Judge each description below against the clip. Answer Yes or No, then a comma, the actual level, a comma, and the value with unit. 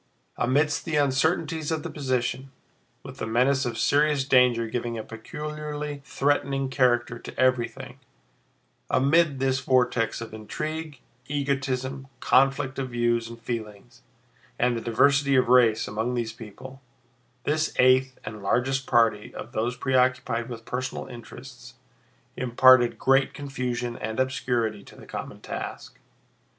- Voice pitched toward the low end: Yes, low, 130 Hz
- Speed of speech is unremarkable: No, slow, 130 wpm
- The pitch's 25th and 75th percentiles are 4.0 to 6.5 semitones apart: No, narrow, 2.6 semitones